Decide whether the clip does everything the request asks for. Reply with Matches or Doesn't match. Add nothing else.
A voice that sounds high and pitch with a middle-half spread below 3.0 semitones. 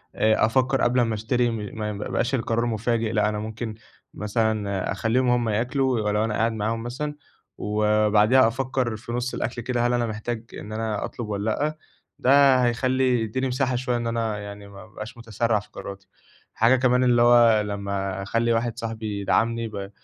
Doesn't match